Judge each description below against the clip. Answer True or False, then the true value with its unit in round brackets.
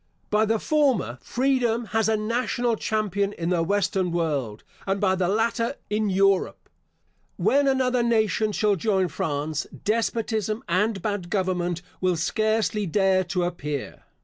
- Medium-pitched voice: False (205 Hz)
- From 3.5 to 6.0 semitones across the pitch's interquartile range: True (3.8 semitones)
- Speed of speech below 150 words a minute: True (140 wpm)